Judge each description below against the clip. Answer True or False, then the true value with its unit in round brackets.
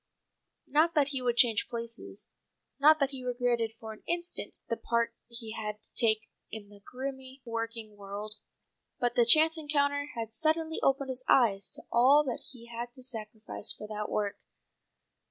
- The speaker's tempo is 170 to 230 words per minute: True (175 wpm)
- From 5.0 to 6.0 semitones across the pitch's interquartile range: False (3.8 semitones)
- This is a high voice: True (240 Hz)